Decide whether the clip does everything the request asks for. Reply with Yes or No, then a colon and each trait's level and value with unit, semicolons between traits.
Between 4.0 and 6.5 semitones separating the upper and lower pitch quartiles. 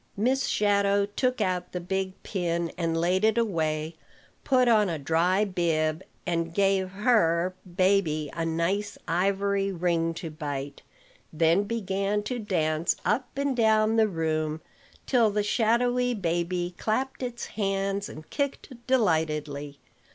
Yes: average, 4.4 semitones